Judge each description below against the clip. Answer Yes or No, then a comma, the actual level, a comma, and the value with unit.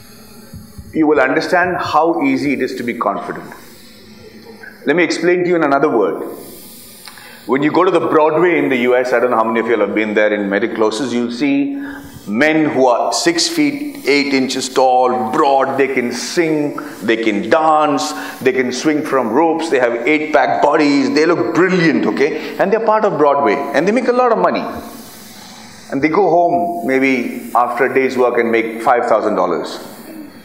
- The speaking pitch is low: No, medium, 150 Hz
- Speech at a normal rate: Yes, average, 195 wpm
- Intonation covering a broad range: Yes, wide, 6.0 semitones